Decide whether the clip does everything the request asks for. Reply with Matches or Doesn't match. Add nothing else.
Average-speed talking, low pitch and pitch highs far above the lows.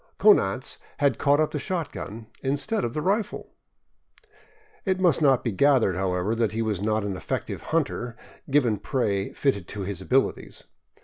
Matches